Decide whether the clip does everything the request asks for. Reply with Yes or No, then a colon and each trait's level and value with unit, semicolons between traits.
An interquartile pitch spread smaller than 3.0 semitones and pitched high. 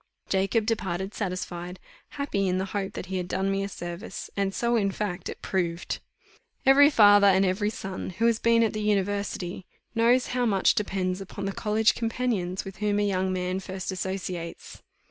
Yes: narrow, 2.4 semitones; high, 195 Hz